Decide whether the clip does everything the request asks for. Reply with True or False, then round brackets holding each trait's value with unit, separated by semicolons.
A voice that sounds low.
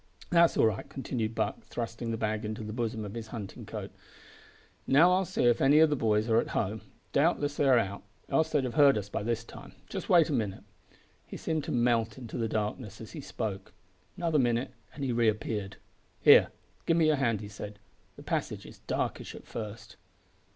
True (115 Hz)